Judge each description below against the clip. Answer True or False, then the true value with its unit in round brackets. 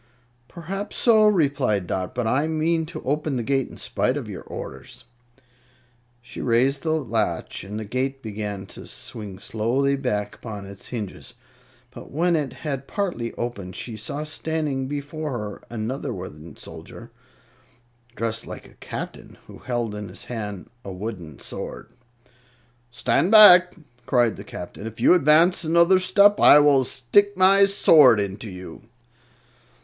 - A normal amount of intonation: False (6.8 semitones)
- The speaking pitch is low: True (130 Hz)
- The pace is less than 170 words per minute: True (150 wpm)